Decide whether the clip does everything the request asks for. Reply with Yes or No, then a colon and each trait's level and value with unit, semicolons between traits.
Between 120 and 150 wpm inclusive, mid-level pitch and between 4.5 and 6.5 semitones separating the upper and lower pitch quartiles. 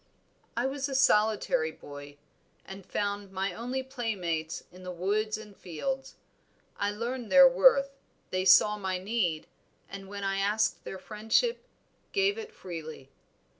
No: average, 140 wpm; high, 205 Hz; average, 5.3 semitones